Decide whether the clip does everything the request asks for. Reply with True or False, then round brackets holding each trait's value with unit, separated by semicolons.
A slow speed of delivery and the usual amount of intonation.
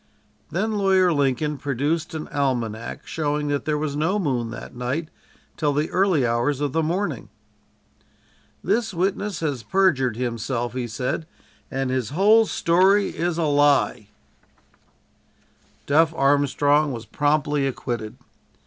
True (130 wpm; 4.5 semitones)